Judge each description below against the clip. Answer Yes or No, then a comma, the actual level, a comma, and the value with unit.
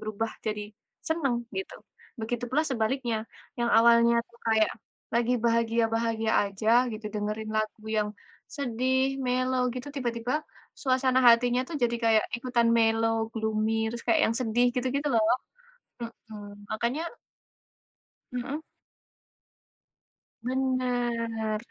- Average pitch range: No, narrow, 2.2 semitones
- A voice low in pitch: No, high, 235 Hz